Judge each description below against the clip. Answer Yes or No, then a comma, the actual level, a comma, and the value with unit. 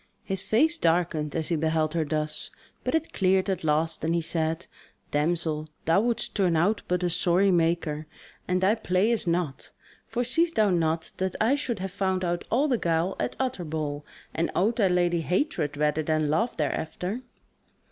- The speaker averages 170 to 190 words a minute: Yes, average, 180 wpm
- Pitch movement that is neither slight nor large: Yes, average, 3.9 semitones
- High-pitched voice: No, medium, 175 Hz